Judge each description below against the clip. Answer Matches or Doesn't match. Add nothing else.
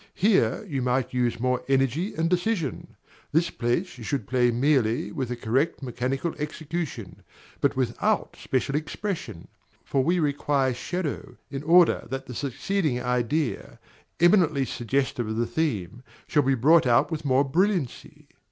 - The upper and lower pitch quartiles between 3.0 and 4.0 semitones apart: Doesn't match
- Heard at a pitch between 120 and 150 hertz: Matches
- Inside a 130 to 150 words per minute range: Matches